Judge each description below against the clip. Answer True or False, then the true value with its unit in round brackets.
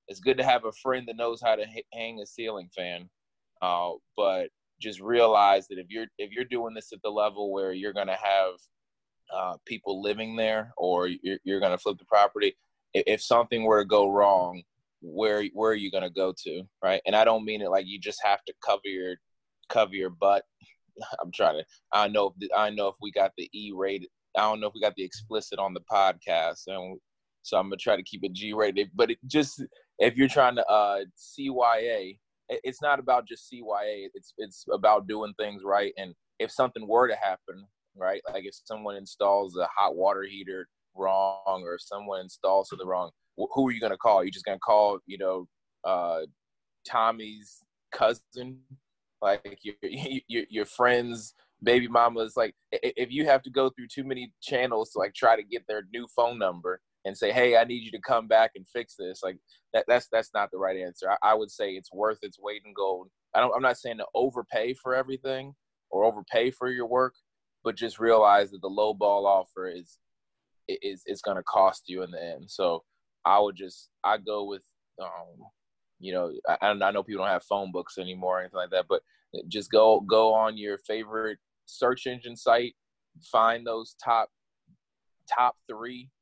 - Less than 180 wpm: False (205 wpm)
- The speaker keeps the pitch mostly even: False (3.8 semitones)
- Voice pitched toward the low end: True (105 Hz)